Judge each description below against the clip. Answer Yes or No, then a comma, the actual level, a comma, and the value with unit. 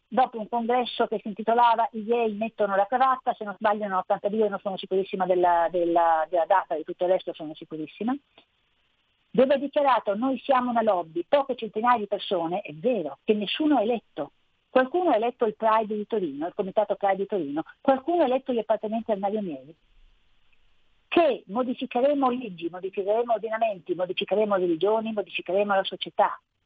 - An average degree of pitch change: Yes, average, 4.5 semitones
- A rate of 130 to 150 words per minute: No, average, 165 wpm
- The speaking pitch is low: No, high, 215 Hz